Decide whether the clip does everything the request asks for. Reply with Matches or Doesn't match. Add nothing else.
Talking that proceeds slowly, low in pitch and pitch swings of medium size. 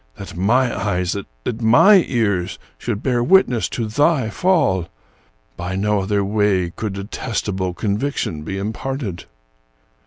Matches